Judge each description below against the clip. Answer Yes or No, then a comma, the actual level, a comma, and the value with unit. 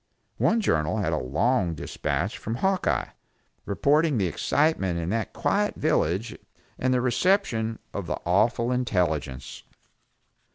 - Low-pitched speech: Yes, low, 115 Hz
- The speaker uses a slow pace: Yes, slow, 125 wpm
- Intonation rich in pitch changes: Yes, wide, 8.3 semitones